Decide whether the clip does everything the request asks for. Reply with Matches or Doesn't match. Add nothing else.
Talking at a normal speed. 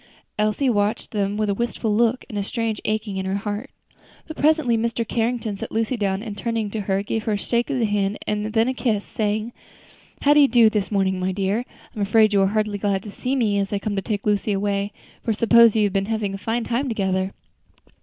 Doesn't match